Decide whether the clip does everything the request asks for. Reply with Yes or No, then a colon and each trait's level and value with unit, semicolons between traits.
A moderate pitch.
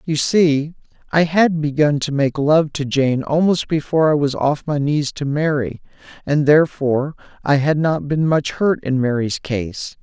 Yes: medium, 145 Hz